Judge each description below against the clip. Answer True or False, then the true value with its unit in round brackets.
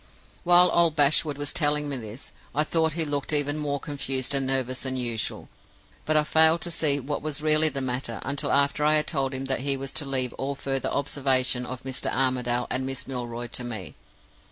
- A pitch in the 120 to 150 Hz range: True (140 Hz)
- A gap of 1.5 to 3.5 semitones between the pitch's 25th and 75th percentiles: True (2.6 semitones)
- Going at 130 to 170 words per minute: False (205 wpm)